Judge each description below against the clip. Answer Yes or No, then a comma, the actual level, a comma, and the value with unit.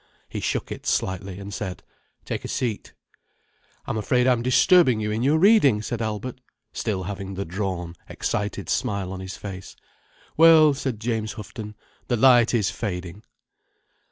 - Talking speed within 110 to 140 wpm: No, average, 155 wpm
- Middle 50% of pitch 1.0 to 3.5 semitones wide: No, average, 4.3 semitones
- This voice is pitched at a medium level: No, low, 105 Hz